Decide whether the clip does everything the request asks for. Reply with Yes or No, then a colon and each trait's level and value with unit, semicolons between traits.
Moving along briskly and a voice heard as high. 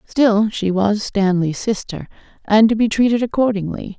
No: average, 150 wpm; high, 210 Hz